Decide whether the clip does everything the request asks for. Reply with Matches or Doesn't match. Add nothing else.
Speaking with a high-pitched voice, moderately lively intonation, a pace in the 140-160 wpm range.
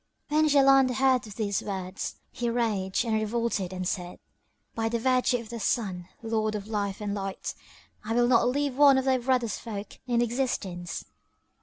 Doesn't match